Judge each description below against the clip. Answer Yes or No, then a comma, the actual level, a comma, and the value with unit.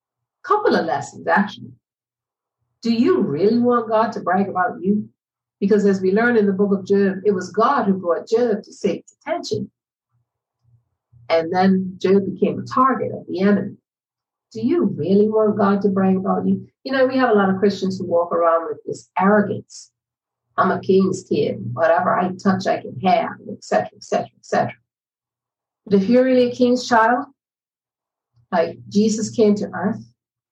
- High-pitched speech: Yes, high, 200 Hz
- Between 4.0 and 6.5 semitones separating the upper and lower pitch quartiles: No, average, 3.5 semitones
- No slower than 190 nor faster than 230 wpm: No, average, 175 wpm